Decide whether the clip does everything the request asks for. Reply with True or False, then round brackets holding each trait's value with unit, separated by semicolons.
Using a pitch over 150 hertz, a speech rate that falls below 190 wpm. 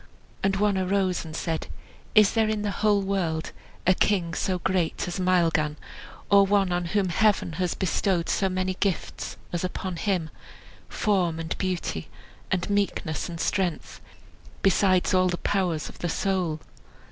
True (185 Hz; 155 wpm)